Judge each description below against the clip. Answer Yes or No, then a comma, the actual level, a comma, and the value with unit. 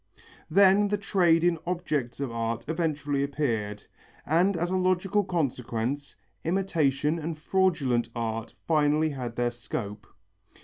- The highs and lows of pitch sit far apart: Yes, wide, 6.5 semitones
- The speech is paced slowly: Yes, slow, 125 wpm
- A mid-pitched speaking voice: Yes, medium, 150 Hz